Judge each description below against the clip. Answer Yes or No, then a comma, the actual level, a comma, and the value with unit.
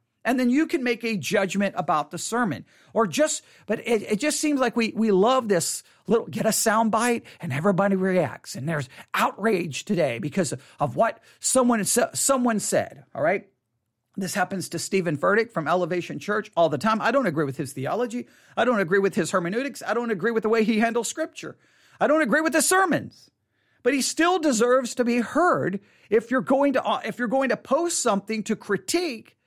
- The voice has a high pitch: Yes, high, 220 Hz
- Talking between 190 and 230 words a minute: Yes, fast, 205 wpm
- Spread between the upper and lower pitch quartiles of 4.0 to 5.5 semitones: Yes, average, 5.1 semitones